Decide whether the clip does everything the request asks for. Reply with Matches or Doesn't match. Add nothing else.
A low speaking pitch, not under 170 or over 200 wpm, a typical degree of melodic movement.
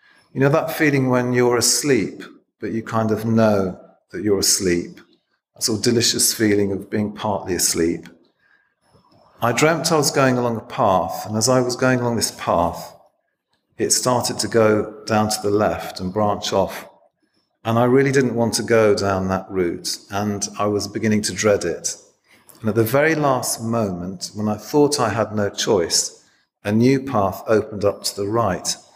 Matches